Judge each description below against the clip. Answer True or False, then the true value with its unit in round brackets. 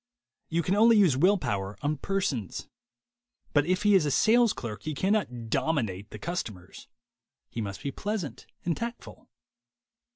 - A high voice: False (155 Hz)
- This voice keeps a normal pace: True (155 wpm)